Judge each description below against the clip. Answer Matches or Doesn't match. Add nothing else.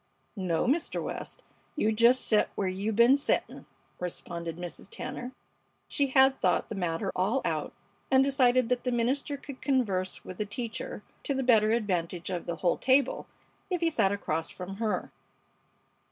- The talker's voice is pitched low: Doesn't match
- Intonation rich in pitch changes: Matches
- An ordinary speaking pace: Matches